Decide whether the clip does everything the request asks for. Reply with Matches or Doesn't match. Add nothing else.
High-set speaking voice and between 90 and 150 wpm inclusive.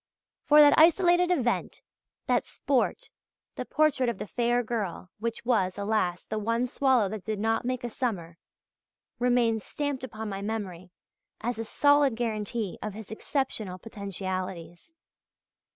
Matches